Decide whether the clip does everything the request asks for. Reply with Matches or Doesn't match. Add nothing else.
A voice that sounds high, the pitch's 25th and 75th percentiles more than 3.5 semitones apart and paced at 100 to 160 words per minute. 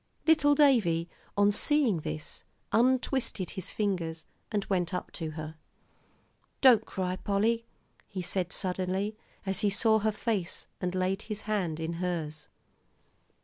Matches